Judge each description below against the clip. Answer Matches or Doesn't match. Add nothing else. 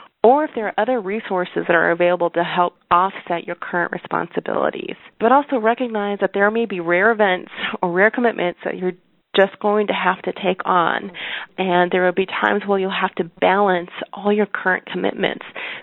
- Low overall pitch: Doesn't match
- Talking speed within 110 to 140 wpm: Doesn't match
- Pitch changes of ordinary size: Matches